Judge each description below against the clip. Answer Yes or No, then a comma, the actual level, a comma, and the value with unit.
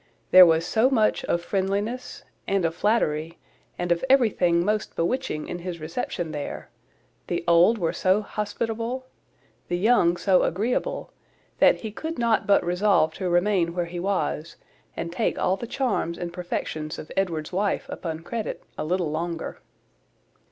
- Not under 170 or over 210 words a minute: No, average, 155 wpm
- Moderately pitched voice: Yes, medium, 180 Hz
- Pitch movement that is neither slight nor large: Yes, average, 3.9 semitones